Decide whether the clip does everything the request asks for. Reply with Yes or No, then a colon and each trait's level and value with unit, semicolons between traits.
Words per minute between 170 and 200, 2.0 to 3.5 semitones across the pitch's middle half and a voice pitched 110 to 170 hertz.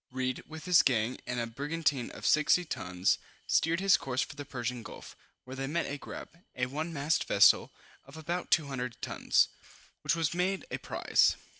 No: average, 180 wpm; average, 4.4 semitones; medium, 140 Hz